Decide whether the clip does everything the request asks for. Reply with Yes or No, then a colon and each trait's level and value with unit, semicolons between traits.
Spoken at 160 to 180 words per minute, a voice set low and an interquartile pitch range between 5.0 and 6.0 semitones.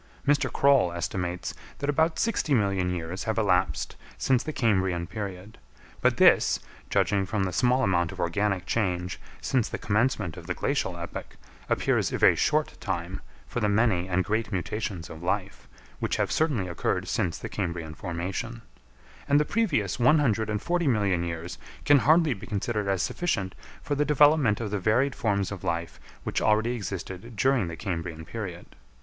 Yes: average, 170 wpm; low, 105 Hz; average, 5.3 semitones